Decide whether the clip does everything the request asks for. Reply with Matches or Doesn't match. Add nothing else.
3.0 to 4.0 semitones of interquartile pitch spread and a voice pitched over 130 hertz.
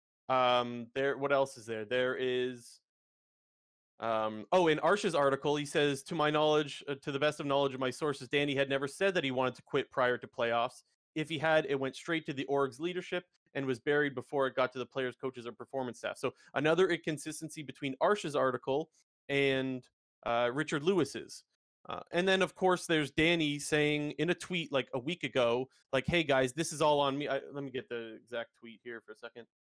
Matches